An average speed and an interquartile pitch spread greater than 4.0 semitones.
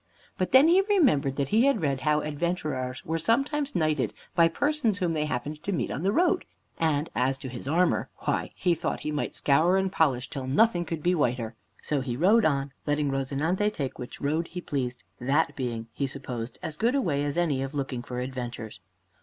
No: fast, 210 wpm; average, 5.2 semitones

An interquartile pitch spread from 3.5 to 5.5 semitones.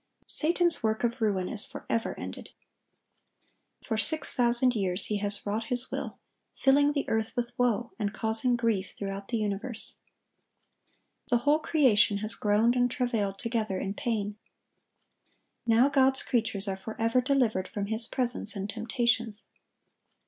No: average, 3.1 semitones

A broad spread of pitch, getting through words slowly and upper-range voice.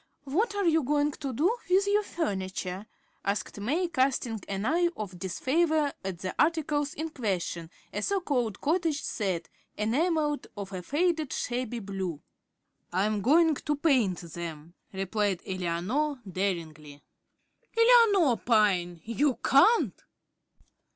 Yes: wide, 8.6 semitones; slow, 130 wpm; high, 245 Hz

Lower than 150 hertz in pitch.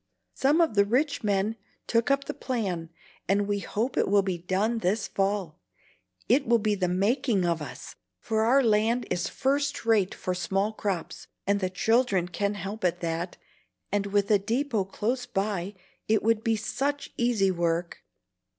No: high, 205 Hz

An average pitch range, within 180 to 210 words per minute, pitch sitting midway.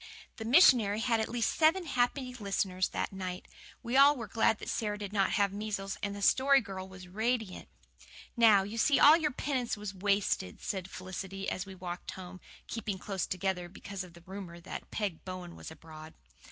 No: average, 3.6 semitones; average, 190 wpm; high, 200 Hz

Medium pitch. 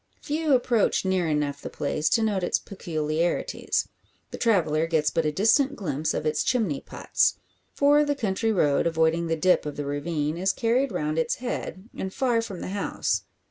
Yes: medium, 180 Hz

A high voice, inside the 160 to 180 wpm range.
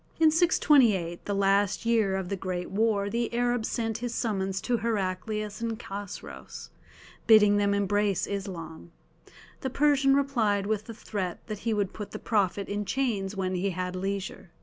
Yes: high, 205 Hz; average, 165 wpm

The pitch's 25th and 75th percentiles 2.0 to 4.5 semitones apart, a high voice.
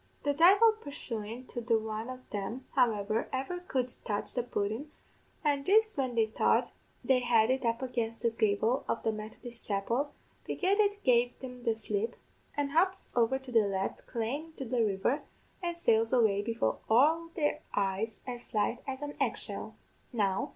Yes: average, 4.2 semitones; high, 245 Hz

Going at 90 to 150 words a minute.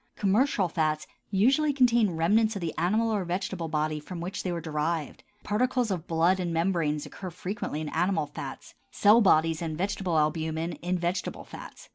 No: average, 170 wpm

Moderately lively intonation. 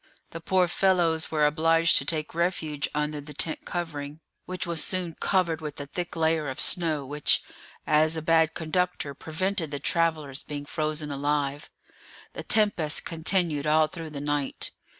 No: narrow, 2.1 semitones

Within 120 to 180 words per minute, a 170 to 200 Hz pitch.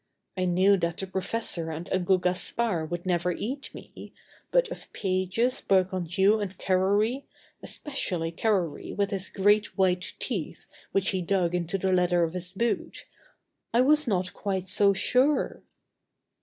Yes: average, 145 wpm; high, 190 Hz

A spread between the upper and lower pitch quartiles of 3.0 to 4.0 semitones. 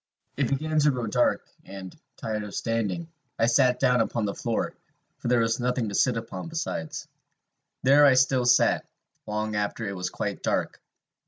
Yes: average, 3.4 semitones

